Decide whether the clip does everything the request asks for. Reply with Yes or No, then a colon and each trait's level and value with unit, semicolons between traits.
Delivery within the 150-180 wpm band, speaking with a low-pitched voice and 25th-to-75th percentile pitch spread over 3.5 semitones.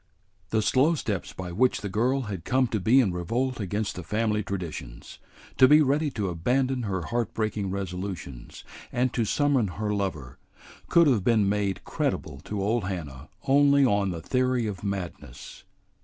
Yes: average, 170 wpm; low, 105 Hz; average, 5.3 semitones